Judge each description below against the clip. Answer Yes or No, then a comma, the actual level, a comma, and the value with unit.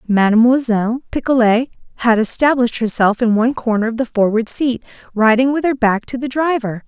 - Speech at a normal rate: Yes, average, 165 wpm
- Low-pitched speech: No, high, 235 Hz